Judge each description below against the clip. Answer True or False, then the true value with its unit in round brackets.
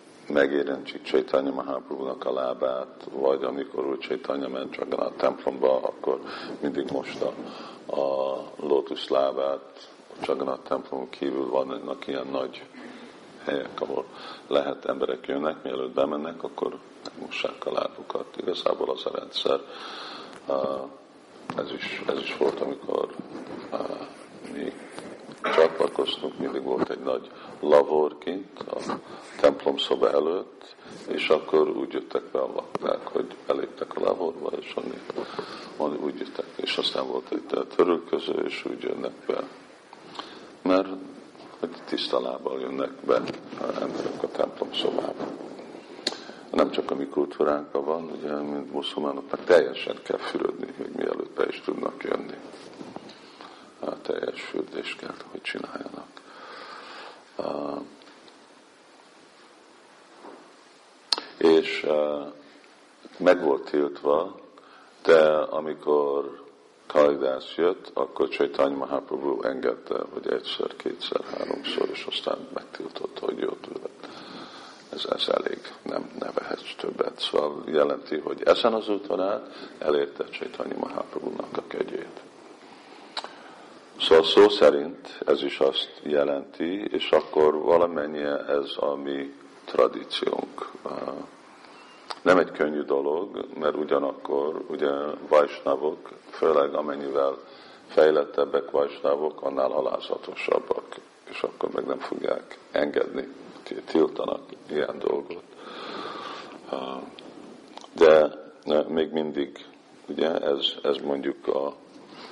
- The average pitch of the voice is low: False (390 Hz)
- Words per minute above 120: False (110 wpm)